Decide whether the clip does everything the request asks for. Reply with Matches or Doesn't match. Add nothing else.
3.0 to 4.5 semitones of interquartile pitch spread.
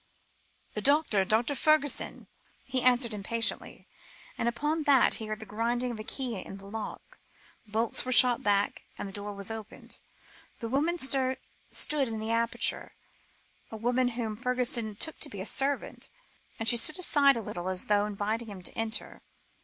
Matches